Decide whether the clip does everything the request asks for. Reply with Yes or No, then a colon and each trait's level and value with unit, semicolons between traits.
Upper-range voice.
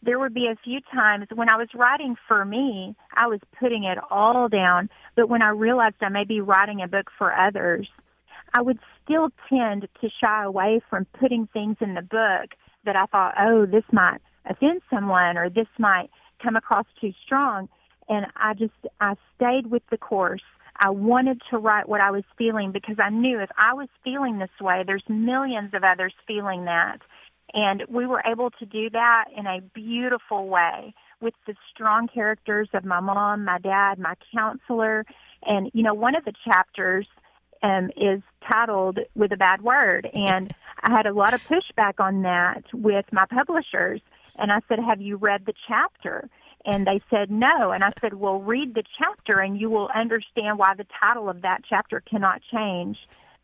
Yes: high, 215 Hz